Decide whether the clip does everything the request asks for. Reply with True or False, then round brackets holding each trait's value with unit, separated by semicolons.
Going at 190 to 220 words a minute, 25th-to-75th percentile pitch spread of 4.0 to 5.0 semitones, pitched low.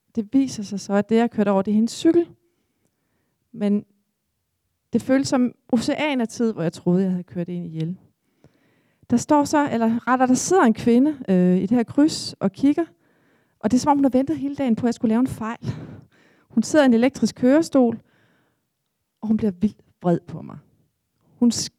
False (210 wpm; 4.6 semitones; 235 Hz)